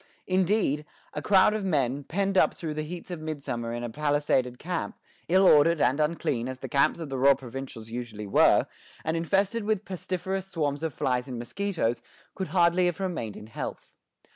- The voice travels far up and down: Yes, wide, 6.0 semitones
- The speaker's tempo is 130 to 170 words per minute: No, average, 185 wpm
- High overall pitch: No, medium, 155 Hz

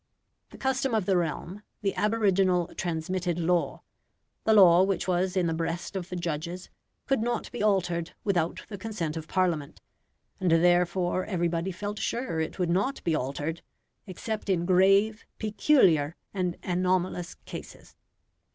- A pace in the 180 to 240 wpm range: No, average, 145 wpm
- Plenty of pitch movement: No, average, 2.7 semitones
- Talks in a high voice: No, medium, 180 Hz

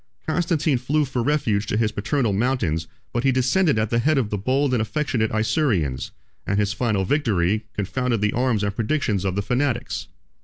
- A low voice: Yes, low, 115 Hz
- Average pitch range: Yes, average, 4.7 semitones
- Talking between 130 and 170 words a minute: No, average, 185 wpm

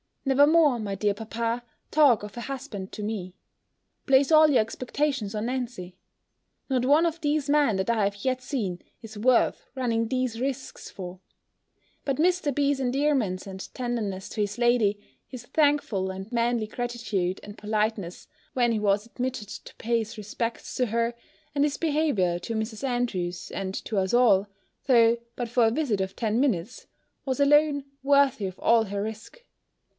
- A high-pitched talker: Yes, high, 235 Hz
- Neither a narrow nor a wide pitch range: Yes, average, 4.4 semitones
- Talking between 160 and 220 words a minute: Yes, average, 170 wpm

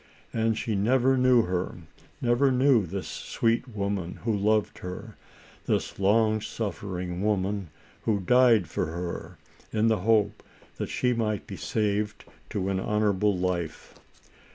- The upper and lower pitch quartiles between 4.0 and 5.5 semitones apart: No, average, 3.2 semitones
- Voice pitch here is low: Yes, low, 105 Hz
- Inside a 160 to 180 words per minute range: No, slow, 135 wpm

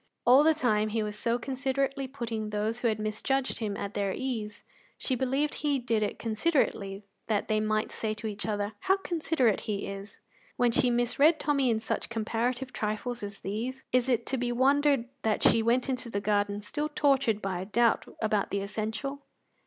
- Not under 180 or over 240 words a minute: Yes, average, 190 wpm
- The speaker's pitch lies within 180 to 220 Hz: No, high, 230 Hz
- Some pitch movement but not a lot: Yes, average, 3.8 semitones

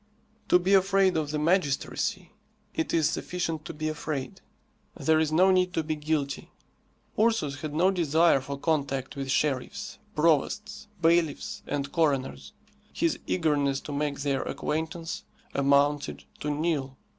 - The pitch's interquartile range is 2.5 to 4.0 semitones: Yes, average, 3.1 semitones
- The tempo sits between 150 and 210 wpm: No, average, 140 wpm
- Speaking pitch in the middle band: Yes, medium, 155 Hz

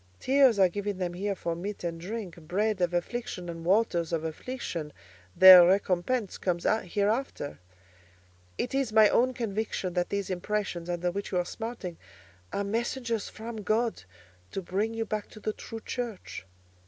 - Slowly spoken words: No, average, 155 wpm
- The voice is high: Yes, high, 200 Hz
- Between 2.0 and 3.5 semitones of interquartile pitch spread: No, average, 4.1 semitones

